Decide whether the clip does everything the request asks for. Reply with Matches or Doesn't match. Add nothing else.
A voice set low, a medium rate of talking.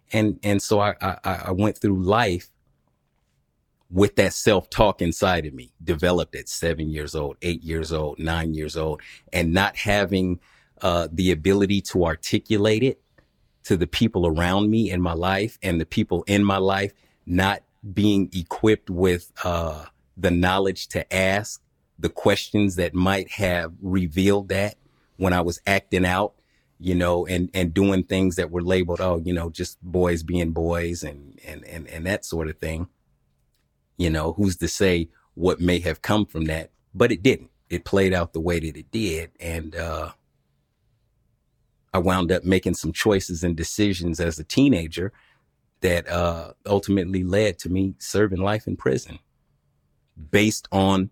Matches